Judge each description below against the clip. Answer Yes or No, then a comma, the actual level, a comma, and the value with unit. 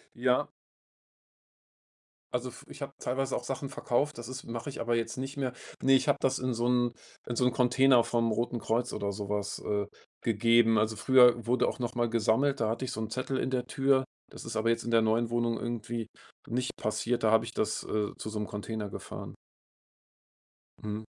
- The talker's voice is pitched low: Yes, low, 120 Hz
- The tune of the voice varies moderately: No, narrow, 2.3 semitones